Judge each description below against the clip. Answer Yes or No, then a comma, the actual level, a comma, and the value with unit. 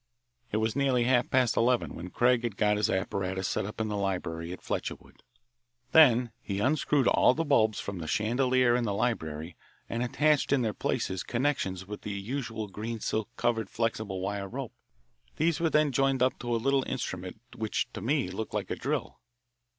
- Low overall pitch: Yes, low, 115 Hz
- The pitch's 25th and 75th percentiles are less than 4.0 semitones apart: No, average, 4.4 semitones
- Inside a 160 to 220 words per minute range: Yes, average, 190 wpm